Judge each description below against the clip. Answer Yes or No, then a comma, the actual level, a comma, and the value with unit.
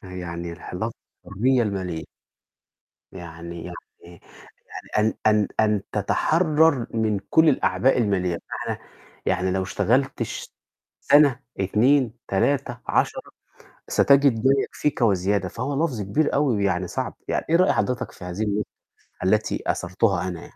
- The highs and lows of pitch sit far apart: Yes, wide, 6.5 semitones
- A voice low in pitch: Yes, low, 105 Hz